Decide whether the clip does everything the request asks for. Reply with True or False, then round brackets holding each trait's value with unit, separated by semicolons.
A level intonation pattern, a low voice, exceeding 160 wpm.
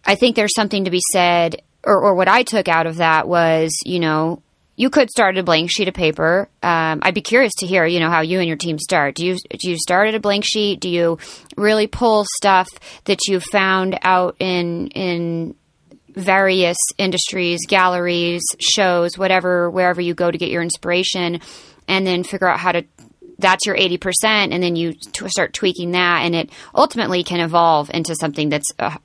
False (2.3 semitones; 180 Hz; 200 wpm)